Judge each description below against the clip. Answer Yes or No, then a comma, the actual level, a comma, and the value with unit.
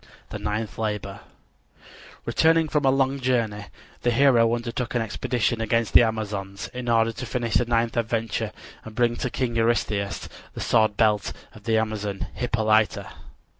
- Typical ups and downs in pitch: No, narrow, 2.1 semitones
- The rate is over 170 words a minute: No, average, 155 wpm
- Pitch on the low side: Yes, low, 115 Hz